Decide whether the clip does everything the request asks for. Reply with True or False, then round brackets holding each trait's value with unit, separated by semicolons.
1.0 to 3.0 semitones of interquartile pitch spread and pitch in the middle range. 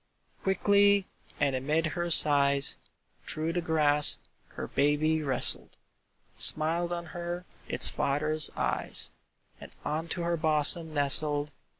True (2.7 semitones; 155 Hz)